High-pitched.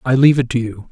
No: low, 125 Hz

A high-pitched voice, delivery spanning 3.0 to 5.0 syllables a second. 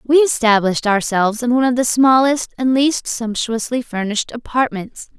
No: high, 240 Hz; 5.2 syllables/s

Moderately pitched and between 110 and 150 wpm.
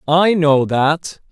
Yes: medium, 155 Hz; slow, 135 wpm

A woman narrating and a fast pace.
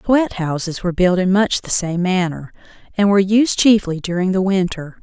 No: female; average, 190 wpm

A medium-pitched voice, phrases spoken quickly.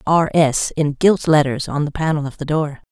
Yes: medium, 150 Hz; fast, 225 wpm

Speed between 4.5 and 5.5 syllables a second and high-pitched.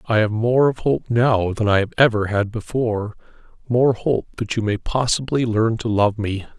No: 4.8 syllables/s; low, 115 Hz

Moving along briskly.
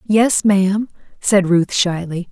No: slow, 130 wpm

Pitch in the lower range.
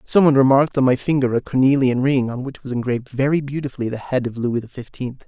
Yes: low, 130 Hz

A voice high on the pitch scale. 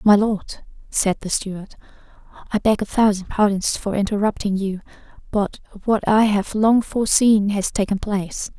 Yes: high, 205 Hz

